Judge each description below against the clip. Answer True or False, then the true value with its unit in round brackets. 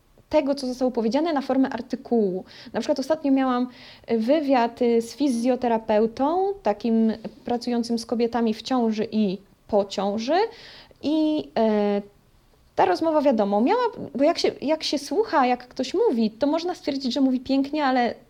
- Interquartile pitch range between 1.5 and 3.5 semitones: False (4.7 semitones)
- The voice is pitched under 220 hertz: False (255 Hz)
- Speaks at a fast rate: False (150 wpm)